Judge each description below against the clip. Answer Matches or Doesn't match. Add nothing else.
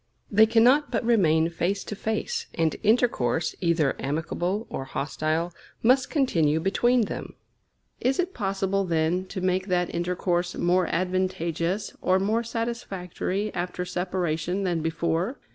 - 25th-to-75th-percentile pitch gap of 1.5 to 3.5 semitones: Doesn't match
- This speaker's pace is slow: Matches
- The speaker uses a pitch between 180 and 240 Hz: Matches